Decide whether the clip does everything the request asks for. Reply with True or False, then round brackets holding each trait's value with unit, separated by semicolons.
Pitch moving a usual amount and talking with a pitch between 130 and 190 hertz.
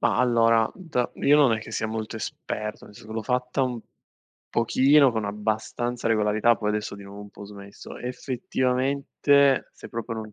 False (3.0 semitones; 115 Hz)